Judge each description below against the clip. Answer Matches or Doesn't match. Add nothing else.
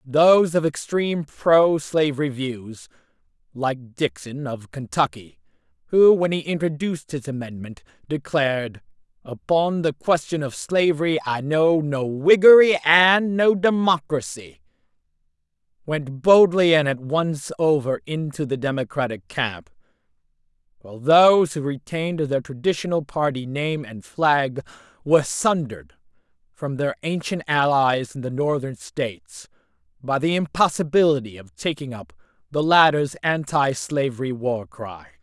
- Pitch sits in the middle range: Matches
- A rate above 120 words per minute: Doesn't match